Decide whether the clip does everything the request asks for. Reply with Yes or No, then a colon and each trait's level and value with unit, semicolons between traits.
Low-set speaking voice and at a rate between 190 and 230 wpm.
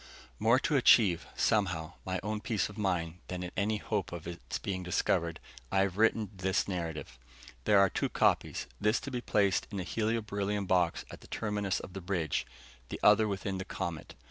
Yes: very low, 95 Hz; average, 195 wpm